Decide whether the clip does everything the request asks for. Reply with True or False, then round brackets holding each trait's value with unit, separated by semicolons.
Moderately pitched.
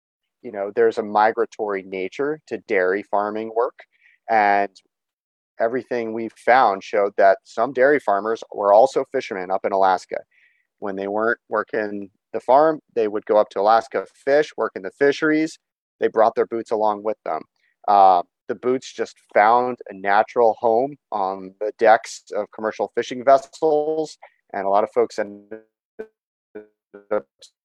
False (110 Hz)